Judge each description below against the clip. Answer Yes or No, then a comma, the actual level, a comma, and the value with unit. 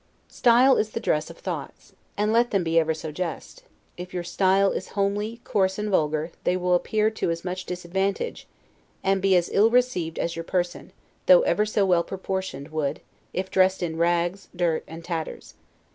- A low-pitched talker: No, medium, 185 Hz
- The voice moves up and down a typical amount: Yes, average, 3.3 semitones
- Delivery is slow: No, average, 185 wpm